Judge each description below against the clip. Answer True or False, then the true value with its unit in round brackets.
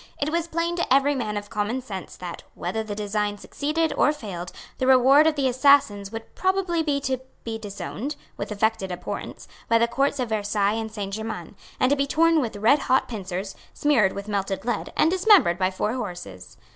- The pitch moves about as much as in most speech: False (5.8 semitones)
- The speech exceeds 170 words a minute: True (195 wpm)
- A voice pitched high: True (225 Hz)